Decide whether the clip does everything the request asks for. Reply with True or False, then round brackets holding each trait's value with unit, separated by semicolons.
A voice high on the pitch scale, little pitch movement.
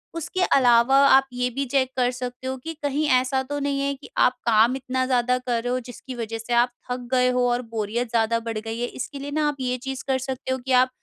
True (250 Hz; 1.7 semitones)